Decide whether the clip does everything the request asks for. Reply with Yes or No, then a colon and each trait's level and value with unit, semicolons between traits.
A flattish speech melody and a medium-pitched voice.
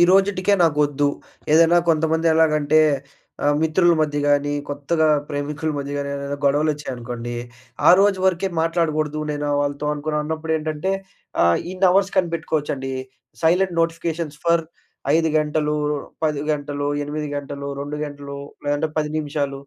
Yes: narrow, 2.3 semitones; medium, 150 Hz